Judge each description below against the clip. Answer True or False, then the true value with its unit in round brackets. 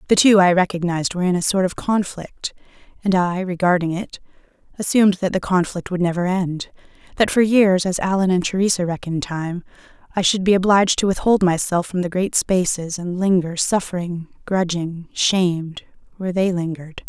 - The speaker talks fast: False (170 wpm)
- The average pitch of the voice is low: False (180 Hz)